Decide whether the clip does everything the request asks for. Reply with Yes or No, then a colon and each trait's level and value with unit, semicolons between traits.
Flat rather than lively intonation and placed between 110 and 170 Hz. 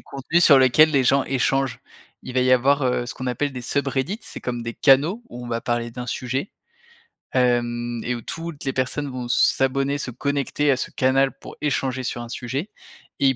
Yes: narrow, 2.2 semitones; low, 130 Hz